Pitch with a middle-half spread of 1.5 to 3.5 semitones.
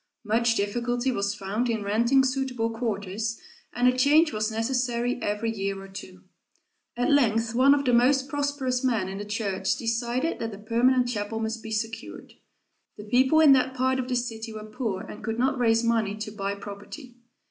Yes: average, 3.1 semitones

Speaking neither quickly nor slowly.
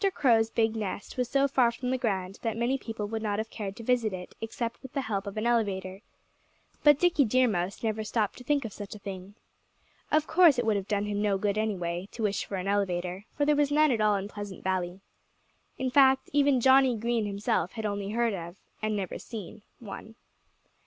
No: fast, 215 wpm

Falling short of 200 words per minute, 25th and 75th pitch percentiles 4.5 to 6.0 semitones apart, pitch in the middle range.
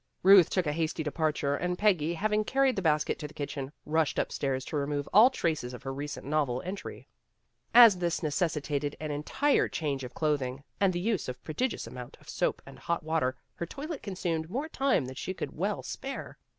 No: fast, 205 wpm; average, 5.2 semitones; medium, 160 Hz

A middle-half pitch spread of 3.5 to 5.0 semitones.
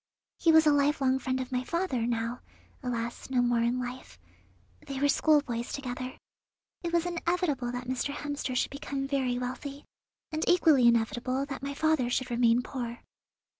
No: average, 2.8 semitones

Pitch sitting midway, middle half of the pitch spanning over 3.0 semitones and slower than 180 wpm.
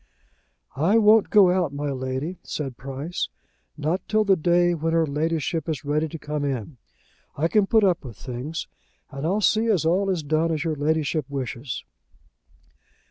Yes: medium, 160 Hz; average, 3.9 semitones; average, 170 wpm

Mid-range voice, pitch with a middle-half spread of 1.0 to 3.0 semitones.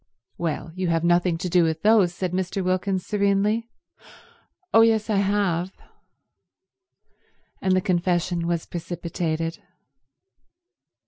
Yes: medium, 180 Hz; narrow, 2.6 semitones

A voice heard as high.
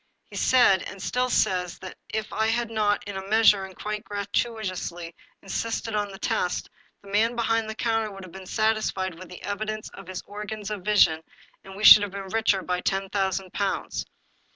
Yes: high, 205 Hz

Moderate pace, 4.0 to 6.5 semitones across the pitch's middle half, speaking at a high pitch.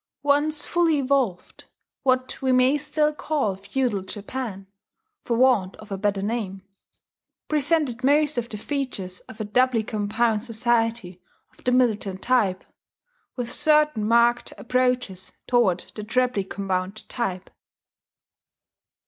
No: slow, 125 wpm; average, 4.3 semitones; high, 235 Hz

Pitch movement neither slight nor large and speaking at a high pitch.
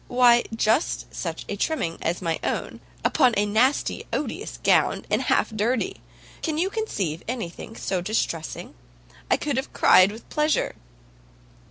No: wide, 6.0 semitones; high, 225 Hz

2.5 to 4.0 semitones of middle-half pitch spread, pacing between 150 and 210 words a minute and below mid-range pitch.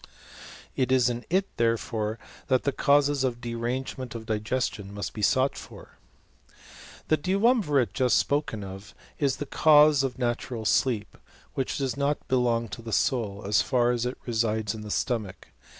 Yes: average, 3.6 semitones; average, 160 wpm; low, 125 Hz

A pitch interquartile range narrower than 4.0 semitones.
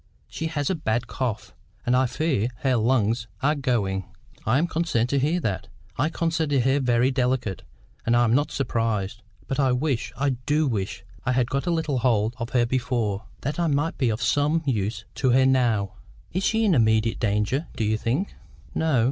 No: average, 4.3 semitones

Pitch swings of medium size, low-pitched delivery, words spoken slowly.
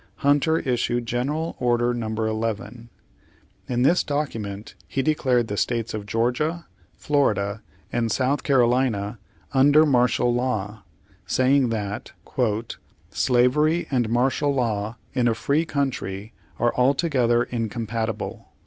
Yes: average, 3.5 semitones; low, 120 Hz; slow, 115 wpm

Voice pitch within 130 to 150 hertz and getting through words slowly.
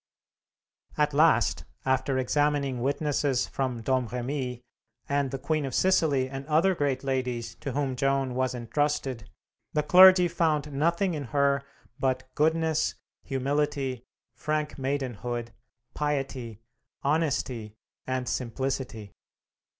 Yes: low, 135 Hz; slow, 110 wpm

